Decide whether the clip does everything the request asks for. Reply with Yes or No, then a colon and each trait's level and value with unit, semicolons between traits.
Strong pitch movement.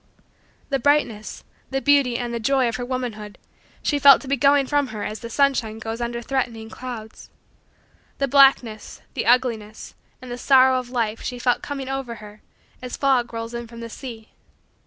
No: average, 2.9 semitones